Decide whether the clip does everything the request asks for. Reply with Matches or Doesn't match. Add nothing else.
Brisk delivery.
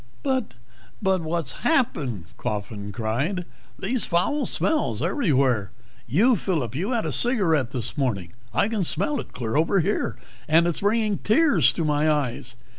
Doesn't match